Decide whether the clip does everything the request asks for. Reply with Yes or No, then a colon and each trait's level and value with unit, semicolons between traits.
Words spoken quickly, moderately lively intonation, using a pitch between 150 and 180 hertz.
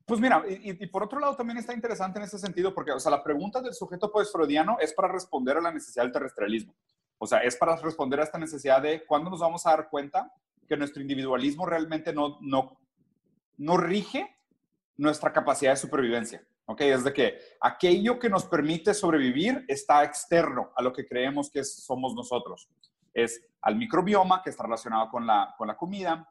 No: fast, 195 wpm; wide, 6.0 semitones; medium, 165 Hz